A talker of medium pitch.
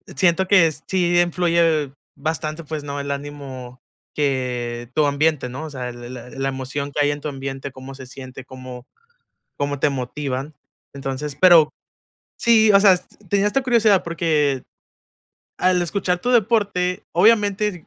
Yes: medium, 150 Hz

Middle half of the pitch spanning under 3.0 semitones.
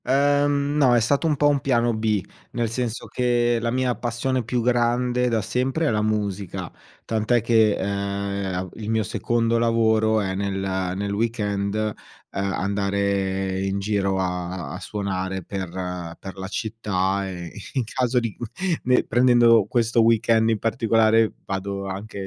No: average, 3.3 semitones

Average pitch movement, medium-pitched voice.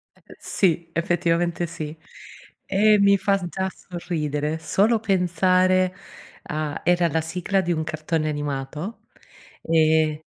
Yes: average, 3.0 semitones; medium, 170 Hz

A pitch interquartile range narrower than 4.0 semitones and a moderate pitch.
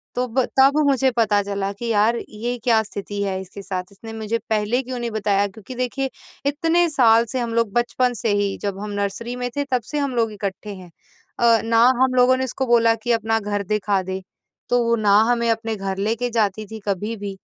No: average, 3.2 semitones; high, 225 Hz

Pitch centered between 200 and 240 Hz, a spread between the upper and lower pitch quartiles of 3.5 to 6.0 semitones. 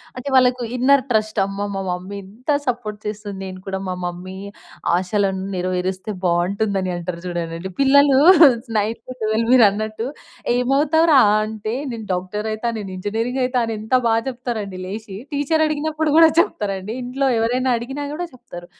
Yes: high, 215 Hz; average, 4.9 semitones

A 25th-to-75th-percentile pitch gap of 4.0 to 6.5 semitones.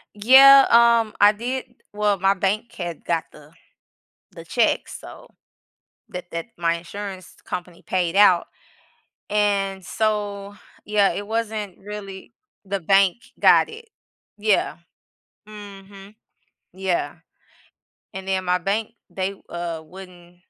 No: narrow, 2.6 semitones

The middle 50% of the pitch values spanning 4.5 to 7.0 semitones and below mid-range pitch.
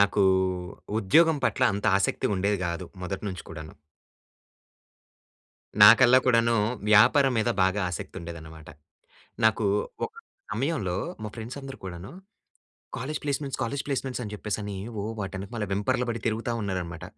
Yes: average, 4.8 semitones; low, 105 Hz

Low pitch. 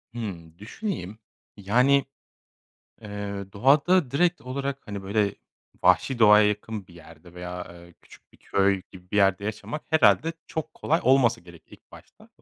Yes: low, 105 Hz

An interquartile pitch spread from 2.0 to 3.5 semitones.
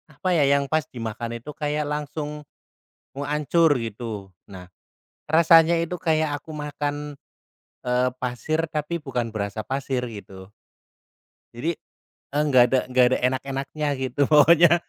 No: average, 3.9 semitones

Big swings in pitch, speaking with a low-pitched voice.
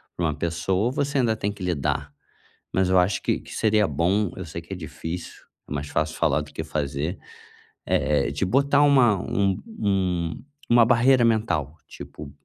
Yes: wide, 6.0 semitones; very low, 95 Hz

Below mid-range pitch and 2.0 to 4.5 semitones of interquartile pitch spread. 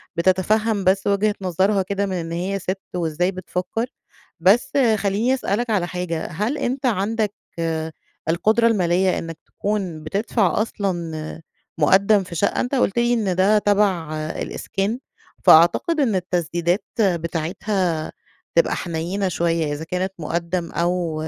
No: medium, 185 Hz; average, 3.5 semitones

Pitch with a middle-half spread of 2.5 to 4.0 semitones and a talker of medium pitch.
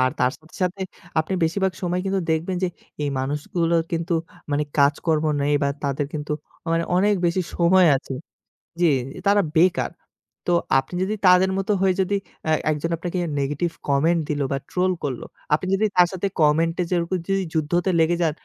Yes: average, 3.6 semitones; medium, 170 Hz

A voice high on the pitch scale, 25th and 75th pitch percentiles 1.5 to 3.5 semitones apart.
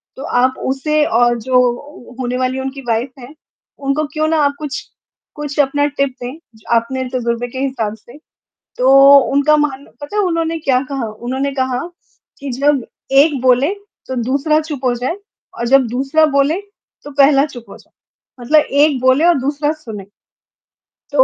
Yes: very high, 270 Hz; average, 2.8 semitones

